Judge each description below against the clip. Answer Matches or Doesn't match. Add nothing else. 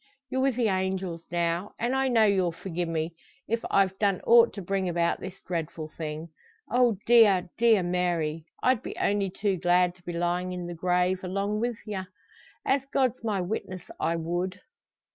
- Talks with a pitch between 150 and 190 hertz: Matches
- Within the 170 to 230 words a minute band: Matches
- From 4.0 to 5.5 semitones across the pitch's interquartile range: Doesn't match